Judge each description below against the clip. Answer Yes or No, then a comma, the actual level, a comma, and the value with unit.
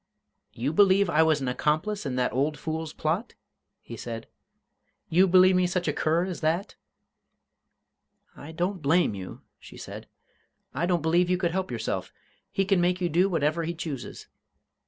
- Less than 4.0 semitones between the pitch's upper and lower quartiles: Yes, average, 3.1 semitones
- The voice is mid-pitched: Yes, medium, 170 Hz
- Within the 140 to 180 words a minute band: Yes, average, 170 wpm